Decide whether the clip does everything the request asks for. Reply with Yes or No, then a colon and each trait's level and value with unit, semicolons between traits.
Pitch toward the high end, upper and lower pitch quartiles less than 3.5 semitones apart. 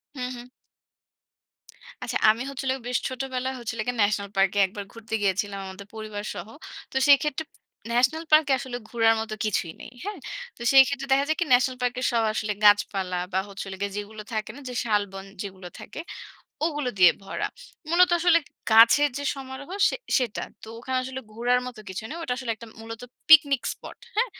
No: high, 240 Hz; average, 4.8 semitones